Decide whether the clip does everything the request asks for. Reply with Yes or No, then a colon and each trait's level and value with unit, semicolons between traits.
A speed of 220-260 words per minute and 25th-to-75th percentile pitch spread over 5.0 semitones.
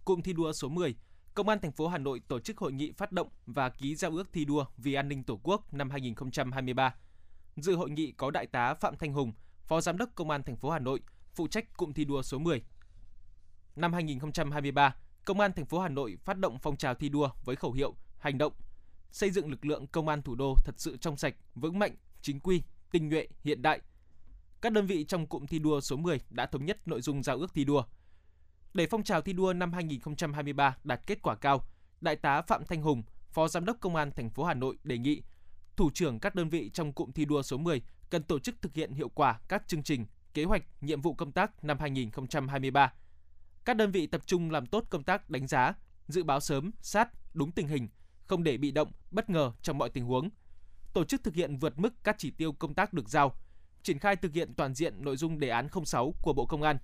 No: average, 235 wpm; average, 4.7 semitones